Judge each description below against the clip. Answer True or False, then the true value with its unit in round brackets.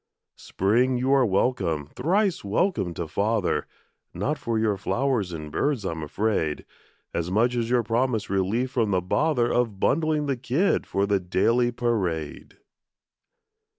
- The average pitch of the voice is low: True (115 Hz)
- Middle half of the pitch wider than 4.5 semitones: True (5.1 semitones)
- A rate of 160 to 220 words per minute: False (145 wpm)